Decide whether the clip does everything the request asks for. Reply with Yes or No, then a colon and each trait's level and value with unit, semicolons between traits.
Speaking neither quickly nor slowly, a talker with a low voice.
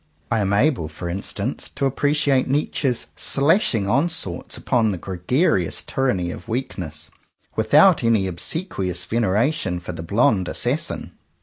No: slow, 130 wpm; low, 110 Hz